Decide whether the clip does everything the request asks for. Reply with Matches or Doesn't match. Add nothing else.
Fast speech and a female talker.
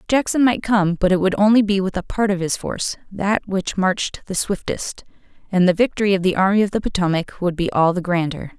Matches